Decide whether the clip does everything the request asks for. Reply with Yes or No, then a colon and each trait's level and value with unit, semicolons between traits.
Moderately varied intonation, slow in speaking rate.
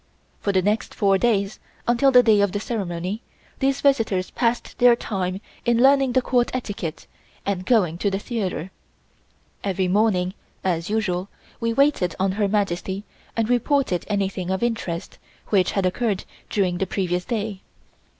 No: average, 4.1 semitones; average, 155 wpm